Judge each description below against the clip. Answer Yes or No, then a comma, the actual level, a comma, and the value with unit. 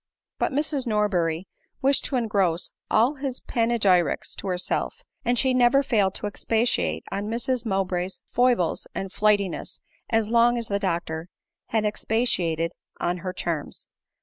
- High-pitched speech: Yes, high, 210 Hz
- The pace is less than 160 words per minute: Yes, average, 145 wpm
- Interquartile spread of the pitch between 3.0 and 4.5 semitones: No, average, 5.0 semitones